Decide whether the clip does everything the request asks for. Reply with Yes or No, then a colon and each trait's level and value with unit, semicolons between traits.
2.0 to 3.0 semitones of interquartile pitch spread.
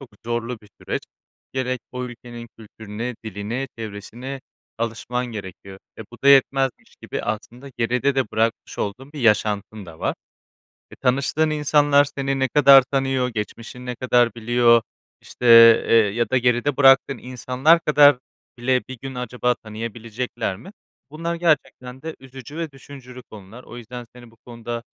Yes: average, 2.7 semitones